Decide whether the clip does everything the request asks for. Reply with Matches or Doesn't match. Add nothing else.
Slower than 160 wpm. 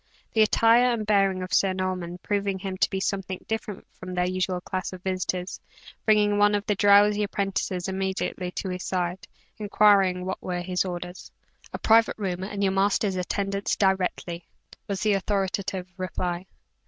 Doesn't match